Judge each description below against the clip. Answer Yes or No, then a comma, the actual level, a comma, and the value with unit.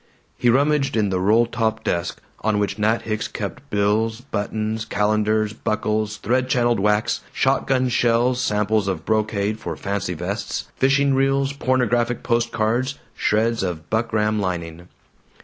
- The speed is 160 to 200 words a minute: No, average, 140 wpm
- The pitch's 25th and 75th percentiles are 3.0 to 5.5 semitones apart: No, narrow, 2.5 semitones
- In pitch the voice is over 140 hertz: No, low, 110 Hz